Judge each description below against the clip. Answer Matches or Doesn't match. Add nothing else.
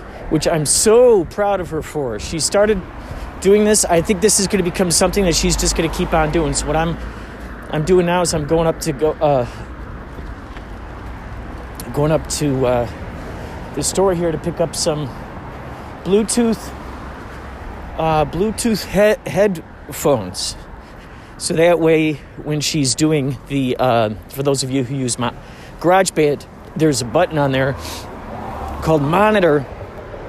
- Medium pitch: Matches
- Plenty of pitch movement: Matches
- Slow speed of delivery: Doesn't match